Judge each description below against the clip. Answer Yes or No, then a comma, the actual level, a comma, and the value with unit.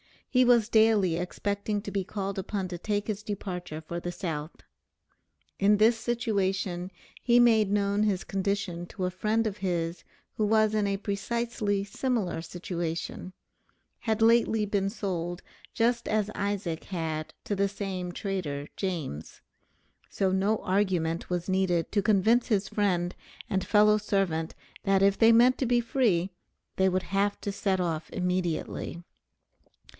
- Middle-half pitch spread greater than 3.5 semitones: No, average, 3.0 semitones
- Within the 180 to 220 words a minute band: No, average, 150 wpm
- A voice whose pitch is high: Yes, high, 195 Hz